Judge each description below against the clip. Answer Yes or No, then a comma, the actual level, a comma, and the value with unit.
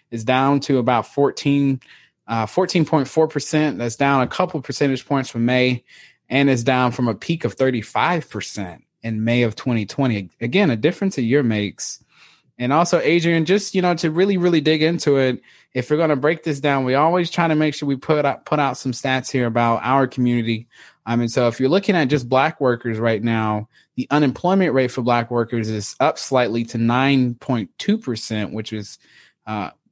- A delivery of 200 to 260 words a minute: No, average, 190 wpm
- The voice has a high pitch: No, low, 130 Hz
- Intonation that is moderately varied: Yes, average, 4.5 semitones